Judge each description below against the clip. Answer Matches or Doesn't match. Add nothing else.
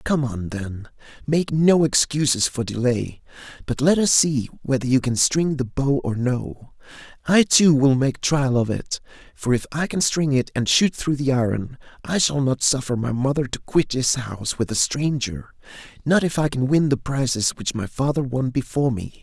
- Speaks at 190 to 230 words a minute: Matches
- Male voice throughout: Matches